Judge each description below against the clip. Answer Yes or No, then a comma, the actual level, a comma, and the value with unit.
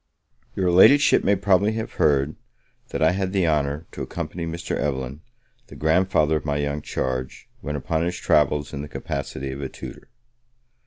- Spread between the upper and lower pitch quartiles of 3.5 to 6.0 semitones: Yes, average, 3.9 semitones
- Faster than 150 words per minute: Yes, average, 170 wpm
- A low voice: Yes, very low, 75 Hz